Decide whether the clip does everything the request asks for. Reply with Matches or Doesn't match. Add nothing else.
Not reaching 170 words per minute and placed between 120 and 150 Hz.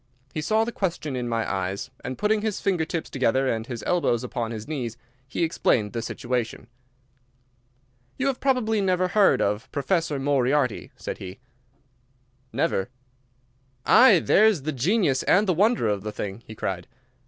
Matches